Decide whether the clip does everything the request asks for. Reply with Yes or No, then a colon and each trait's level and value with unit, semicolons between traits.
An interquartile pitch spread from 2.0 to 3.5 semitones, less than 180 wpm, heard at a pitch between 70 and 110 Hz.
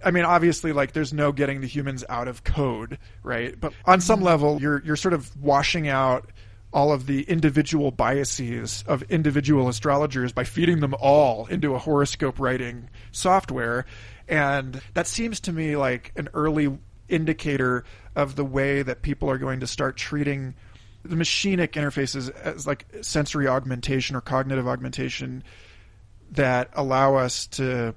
No: average, 3.0 semitones; average, 155 wpm; low, 135 Hz